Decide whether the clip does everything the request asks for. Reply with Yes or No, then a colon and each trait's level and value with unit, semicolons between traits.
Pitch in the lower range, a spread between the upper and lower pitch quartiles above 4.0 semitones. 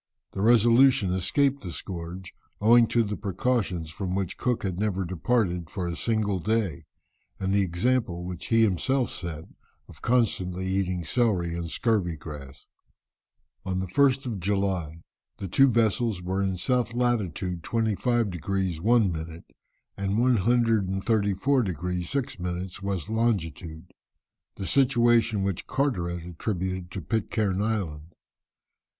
Yes: very low, 95 Hz; average, 4.5 semitones